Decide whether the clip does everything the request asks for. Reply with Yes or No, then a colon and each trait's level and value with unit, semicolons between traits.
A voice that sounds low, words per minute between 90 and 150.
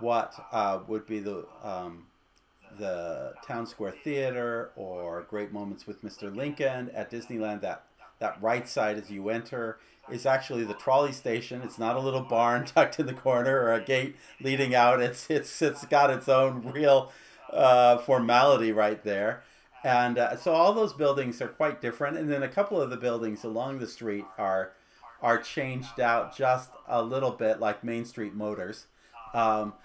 No: low, 120 Hz; average, 175 wpm